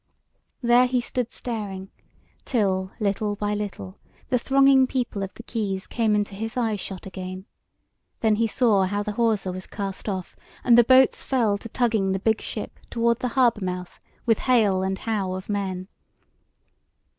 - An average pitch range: Yes, average, 3.6 semitones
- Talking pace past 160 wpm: Yes, average, 170 wpm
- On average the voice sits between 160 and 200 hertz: No, high, 210 Hz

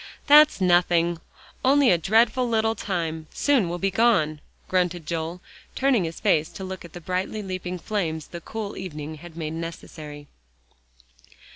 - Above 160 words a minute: No, average, 150 wpm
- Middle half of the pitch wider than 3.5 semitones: Yes, average, 4.7 semitones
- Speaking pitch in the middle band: Yes, medium, 180 Hz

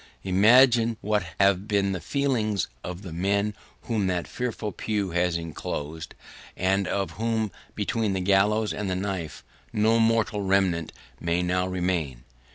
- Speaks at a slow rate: No, average, 145 wpm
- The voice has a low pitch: Yes, low, 100 Hz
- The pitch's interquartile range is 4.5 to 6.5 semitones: No, average, 3.0 semitones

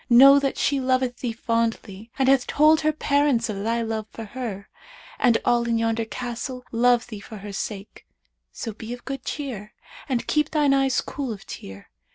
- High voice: Yes, high, 240 Hz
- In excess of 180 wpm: Yes, average, 190 wpm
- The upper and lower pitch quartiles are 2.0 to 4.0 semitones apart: Yes, average, 3.1 semitones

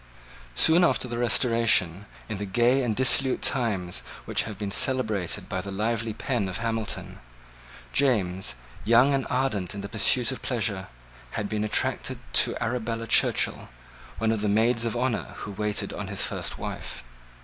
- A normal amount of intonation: Yes, average, 3.1 semitones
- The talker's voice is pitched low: Yes, low, 115 Hz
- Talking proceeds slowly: No, average, 160 wpm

